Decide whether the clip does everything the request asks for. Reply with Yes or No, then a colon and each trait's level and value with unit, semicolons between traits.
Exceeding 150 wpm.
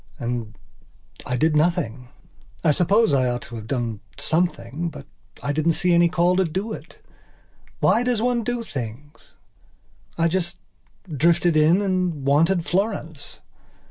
No: average, 140 wpm